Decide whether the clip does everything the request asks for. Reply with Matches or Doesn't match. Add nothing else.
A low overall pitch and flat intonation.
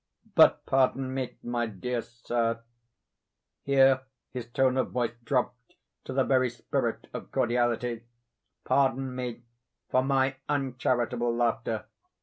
Matches